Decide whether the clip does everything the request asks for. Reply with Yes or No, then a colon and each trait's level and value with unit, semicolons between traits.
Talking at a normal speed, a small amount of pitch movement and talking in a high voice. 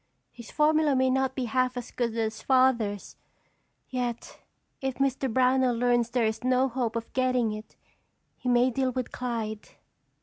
Yes: average, 160 wpm; narrow, 2.0 semitones; very high, 250 Hz